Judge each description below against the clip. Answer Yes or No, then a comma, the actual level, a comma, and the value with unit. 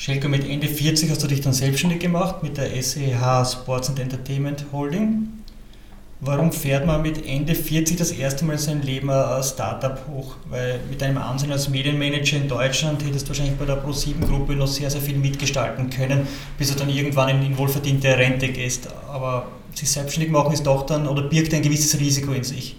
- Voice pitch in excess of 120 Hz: Yes, medium, 140 Hz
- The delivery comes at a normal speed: No, fast, 195 wpm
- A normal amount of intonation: No, narrow, 1.7 semitones